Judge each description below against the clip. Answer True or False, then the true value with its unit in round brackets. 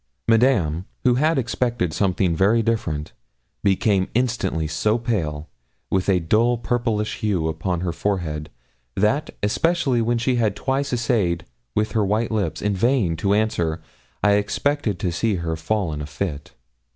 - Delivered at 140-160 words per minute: True (150 wpm)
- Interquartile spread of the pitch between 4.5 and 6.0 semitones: True (5.4 semitones)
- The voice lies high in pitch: False (105 Hz)